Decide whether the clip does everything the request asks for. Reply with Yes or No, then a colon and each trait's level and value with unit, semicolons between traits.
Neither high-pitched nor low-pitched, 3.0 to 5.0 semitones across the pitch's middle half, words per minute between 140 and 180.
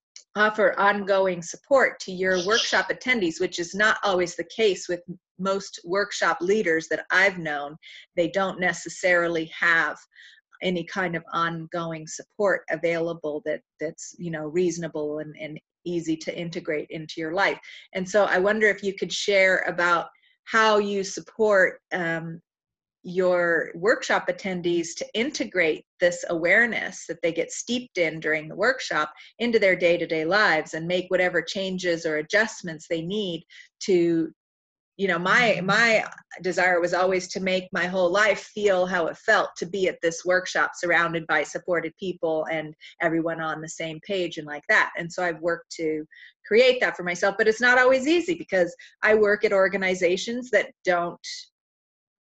Yes: medium, 180 Hz; average, 3.3 semitones; average, 160 wpm